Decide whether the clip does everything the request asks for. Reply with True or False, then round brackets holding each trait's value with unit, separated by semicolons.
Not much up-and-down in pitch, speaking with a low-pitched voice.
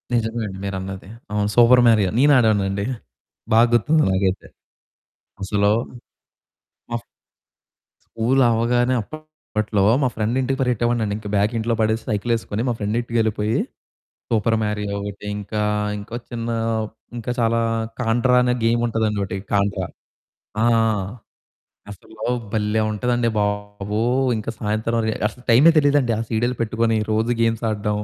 True (2.3 semitones; 110 Hz)